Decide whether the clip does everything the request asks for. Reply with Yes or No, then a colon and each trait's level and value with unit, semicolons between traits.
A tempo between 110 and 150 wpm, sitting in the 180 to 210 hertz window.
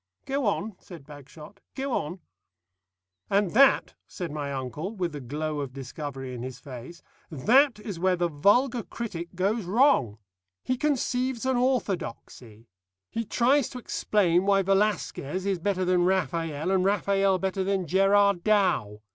Yes: average, 145 wpm; medium, 185 Hz